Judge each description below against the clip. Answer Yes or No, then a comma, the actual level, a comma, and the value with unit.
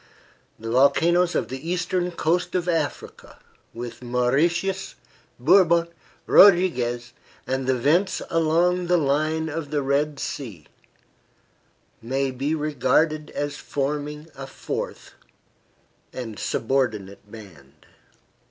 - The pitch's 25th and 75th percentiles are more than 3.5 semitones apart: Yes, average, 4.9 semitones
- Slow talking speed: Yes, slow, 105 wpm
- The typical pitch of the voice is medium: Yes, medium, 145 Hz